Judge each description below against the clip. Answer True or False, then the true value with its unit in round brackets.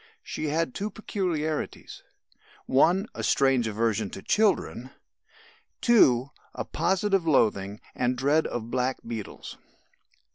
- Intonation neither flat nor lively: False (6.9 semitones)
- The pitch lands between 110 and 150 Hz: True (135 Hz)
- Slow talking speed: True (105 wpm)